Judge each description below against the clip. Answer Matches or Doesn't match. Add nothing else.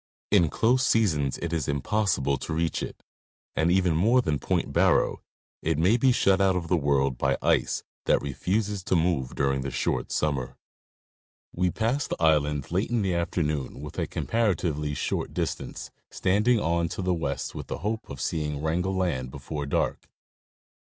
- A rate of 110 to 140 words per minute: Doesn't match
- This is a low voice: Matches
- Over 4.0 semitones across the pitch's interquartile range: Matches